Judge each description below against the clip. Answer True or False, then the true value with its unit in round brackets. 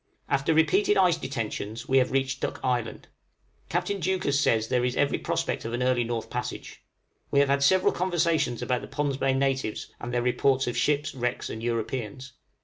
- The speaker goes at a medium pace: True (185 wpm)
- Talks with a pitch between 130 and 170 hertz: True (135 Hz)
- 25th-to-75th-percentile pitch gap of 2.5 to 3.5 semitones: True (3.0 semitones)